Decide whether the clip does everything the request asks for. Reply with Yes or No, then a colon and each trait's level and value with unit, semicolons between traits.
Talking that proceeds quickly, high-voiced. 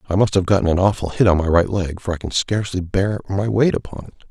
No: fast, 280 wpm; very low, 95 Hz